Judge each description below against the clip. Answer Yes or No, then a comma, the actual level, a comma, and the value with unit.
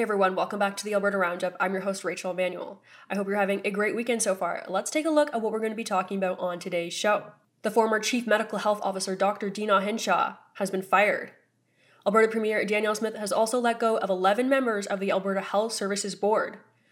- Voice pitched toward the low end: No, high, 205 Hz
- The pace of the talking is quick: Yes, fast, 230 wpm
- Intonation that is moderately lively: No, narrow, 2.3 semitones